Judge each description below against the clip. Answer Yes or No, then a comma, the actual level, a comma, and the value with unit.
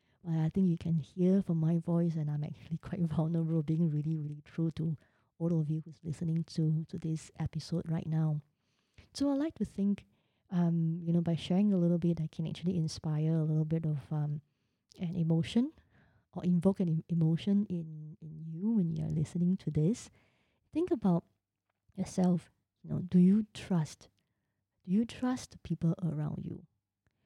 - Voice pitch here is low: No, medium, 165 Hz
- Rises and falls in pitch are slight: Yes, narrow, 2.3 semitones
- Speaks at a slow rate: No, average, 175 wpm